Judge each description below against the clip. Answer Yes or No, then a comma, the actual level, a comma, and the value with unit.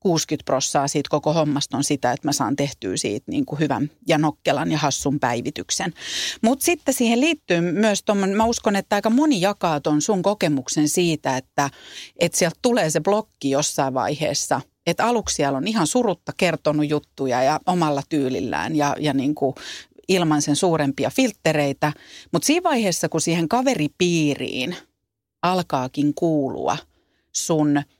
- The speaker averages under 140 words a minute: No, fast, 155 wpm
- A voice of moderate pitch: Yes, medium, 155 Hz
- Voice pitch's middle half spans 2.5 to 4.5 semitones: No, average, 5.3 semitones